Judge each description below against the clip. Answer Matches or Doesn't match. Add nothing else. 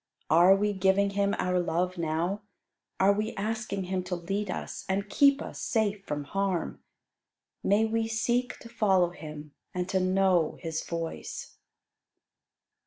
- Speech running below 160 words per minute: Matches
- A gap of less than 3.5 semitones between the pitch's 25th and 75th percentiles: Matches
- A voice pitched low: Doesn't match